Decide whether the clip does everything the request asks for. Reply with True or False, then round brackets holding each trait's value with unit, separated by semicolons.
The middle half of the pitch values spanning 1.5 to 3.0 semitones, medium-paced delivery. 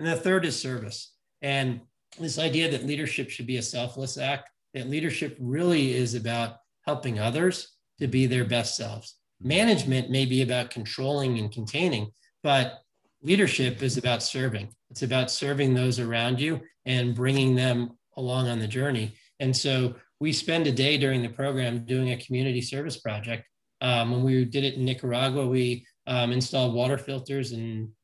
True (2.4 semitones; 170 wpm)